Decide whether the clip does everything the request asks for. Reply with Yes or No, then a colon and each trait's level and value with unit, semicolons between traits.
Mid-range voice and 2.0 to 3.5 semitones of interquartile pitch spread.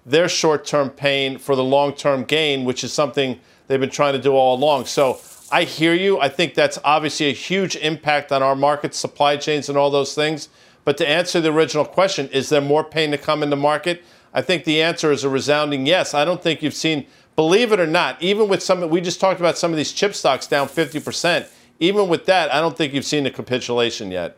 Yes: medium, 150 Hz; average, 2.9 semitones